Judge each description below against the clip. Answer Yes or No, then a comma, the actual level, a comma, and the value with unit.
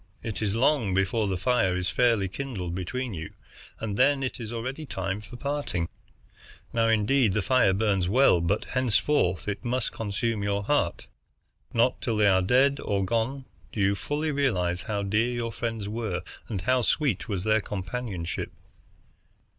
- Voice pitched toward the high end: No, low, 110 Hz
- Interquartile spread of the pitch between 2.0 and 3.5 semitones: No, average, 4.4 semitones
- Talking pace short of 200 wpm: Yes, average, 165 wpm